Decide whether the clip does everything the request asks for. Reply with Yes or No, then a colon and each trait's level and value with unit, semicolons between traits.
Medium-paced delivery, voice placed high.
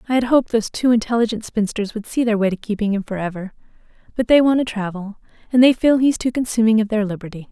No: fast, 230 wpm; high, 220 Hz